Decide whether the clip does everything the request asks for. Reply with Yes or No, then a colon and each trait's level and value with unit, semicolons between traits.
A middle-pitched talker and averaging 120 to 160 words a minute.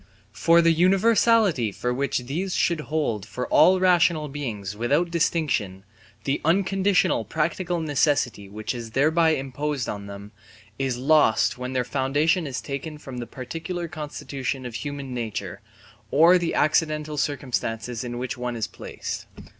Yes: medium, 145 Hz; average, 145 wpm